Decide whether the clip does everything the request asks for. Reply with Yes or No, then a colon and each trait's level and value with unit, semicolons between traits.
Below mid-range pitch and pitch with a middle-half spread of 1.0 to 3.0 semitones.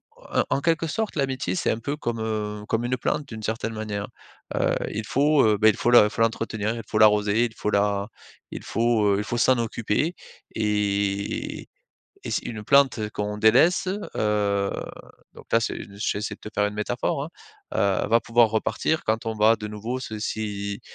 Yes: low, 110 Hz; narrow, 2.4 semitones